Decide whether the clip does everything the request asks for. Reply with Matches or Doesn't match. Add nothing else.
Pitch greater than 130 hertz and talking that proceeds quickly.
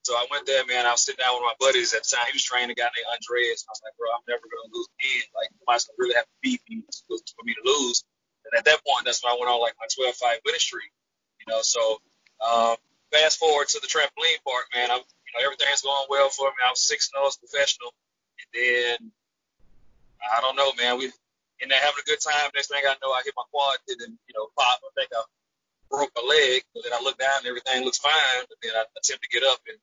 Matches